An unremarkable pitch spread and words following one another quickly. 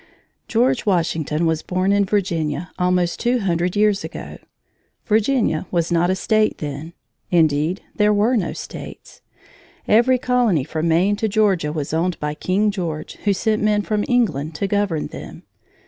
No: average, 4.5 semitones; average, 155 wpm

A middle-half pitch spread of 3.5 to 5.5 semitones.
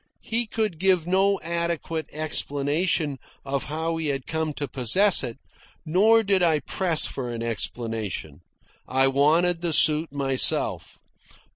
Yes: average, 4.3 semitones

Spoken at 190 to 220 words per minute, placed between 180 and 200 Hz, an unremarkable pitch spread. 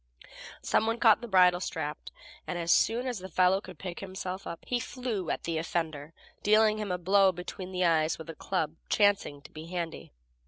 Yes: average, 200 wpm; medium, 185 Hz; average, 3.4 semitones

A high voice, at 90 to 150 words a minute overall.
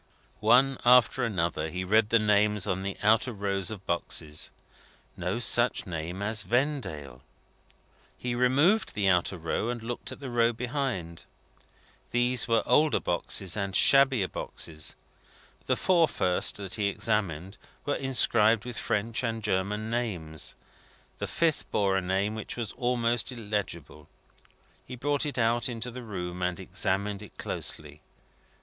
No: low, 105 Hz; average, 145 wpm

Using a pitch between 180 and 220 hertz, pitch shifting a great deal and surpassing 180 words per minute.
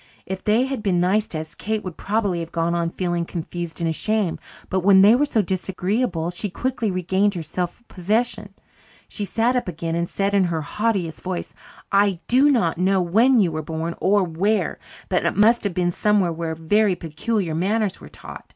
No: high, 190 Hz; average, 3.8 semitones; average, 195 wpm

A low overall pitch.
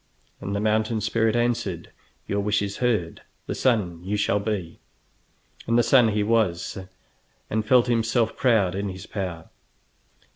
Yes: low, 105 Hz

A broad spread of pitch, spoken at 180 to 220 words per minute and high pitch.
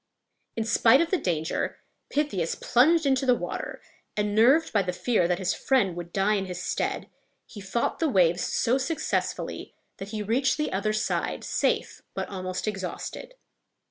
No: wide, 6.2 semitones; average, 170 wpm; high, 210 Hz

